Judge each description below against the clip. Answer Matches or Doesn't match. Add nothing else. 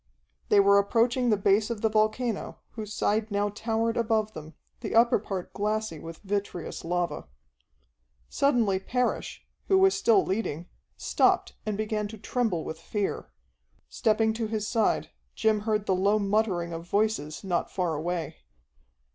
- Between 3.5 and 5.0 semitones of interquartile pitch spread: Doesn't match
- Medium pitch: Doesn't match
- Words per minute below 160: Matches